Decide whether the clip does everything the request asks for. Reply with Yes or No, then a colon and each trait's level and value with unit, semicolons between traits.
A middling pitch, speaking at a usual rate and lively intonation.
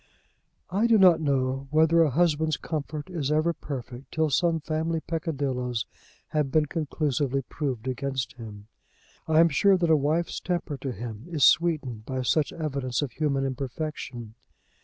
No: medium, 150 Hz; average, 155 wpm; average, 3.5 semitones